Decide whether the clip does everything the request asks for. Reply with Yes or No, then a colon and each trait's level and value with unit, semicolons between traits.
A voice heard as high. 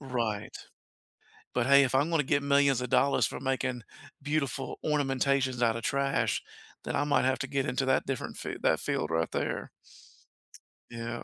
No: low, 135 Hz